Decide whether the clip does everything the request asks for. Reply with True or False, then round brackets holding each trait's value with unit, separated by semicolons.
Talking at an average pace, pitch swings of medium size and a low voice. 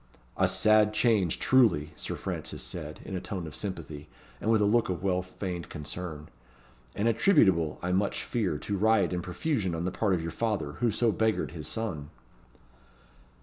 True (180 wpm; 4.4 semitones; 95 Hz)